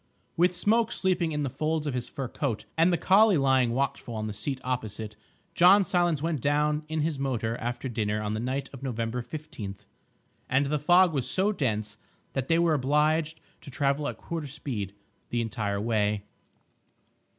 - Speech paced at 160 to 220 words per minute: Yes, average, 180 wpm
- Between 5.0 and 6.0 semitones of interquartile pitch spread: Yes, wide, 5.4 semitones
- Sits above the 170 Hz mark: No, medium, 140 Hz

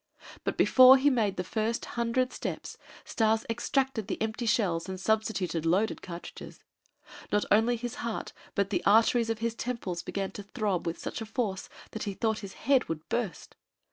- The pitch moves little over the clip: No, average, 3.4 semitones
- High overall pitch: Yes, high, 220 Hz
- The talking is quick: No, average, 180 wpm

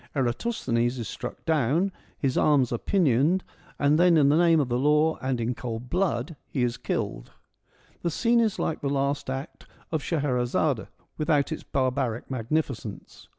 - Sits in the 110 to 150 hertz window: Yes, medium, 140 Hz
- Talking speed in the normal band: Yes, average, 170 wpm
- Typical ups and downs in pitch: Yes, average, 4.4 semitones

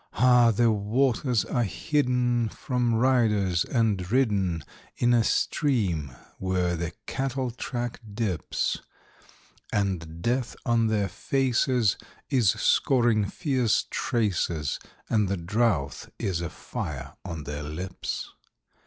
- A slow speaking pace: Yes, slow, 110 wpm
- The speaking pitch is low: Yes, low, 110 Hz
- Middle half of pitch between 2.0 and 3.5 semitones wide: No, average, 4.9 semitones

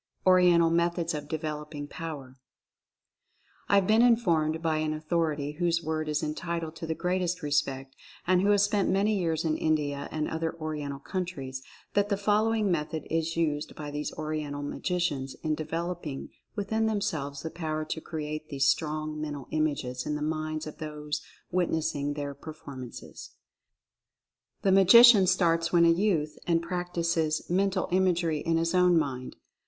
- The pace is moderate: Yes, average, 160 wpm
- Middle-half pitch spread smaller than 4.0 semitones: Yes, average, 2.9 semitones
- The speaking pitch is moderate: Yes, medium, 160 Hz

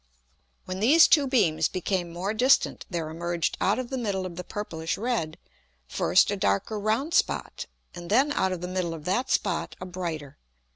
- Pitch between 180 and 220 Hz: Yes, medium, 185 Hz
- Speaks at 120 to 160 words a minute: No, average, 185 wpm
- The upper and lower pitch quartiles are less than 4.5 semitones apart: No, average, 4.8 semitones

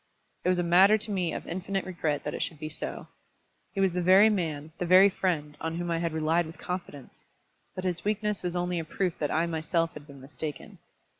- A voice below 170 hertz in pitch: No, medium, 175 Hz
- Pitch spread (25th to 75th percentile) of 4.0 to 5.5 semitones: No, average, 2.8 semitones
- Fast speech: Yes, fast, 225 wpm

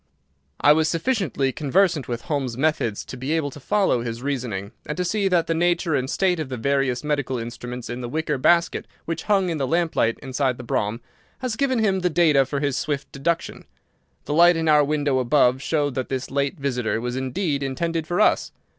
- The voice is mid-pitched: Yes, medium, 145 Hz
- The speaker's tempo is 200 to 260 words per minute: Yes, fast, 205 wpm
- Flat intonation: No, average, 4.6 semitones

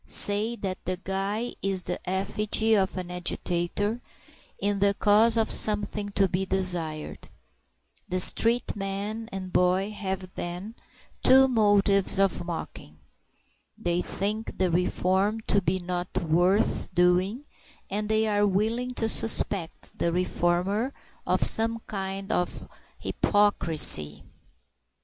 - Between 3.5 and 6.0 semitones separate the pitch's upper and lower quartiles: No, average, 2.9 semitones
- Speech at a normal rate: No, slow, 120 wpm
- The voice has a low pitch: No, high, 195 Hz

